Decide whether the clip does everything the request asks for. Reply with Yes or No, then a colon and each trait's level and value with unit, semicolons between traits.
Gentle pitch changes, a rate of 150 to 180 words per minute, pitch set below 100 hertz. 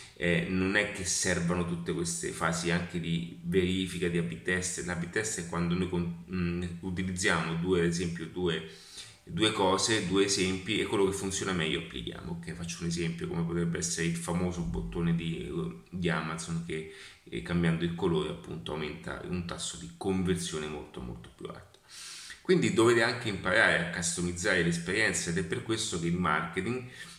Yes: narrow, 1.8 semitones; average, 165 wpm; very low, 90 Hz